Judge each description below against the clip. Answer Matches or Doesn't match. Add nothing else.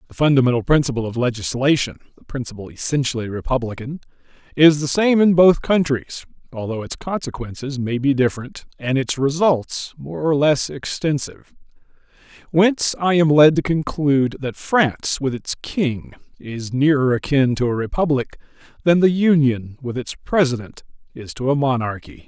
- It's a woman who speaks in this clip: Doesn't match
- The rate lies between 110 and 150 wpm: Matches